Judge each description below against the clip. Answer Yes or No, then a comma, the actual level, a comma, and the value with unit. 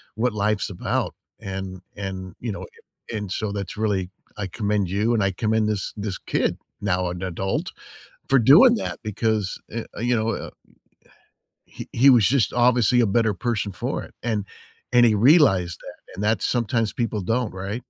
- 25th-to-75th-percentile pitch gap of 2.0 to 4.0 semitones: Yes, average, 3.4 semitones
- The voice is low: Yes, low, 105 Hz